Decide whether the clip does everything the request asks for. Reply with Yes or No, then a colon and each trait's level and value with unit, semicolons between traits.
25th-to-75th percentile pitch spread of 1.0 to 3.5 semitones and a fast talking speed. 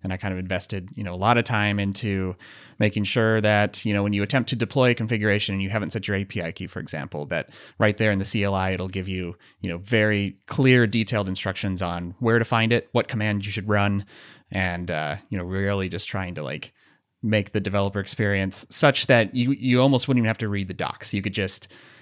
Yes: average, 2.9 semitones; fast, 235 wpm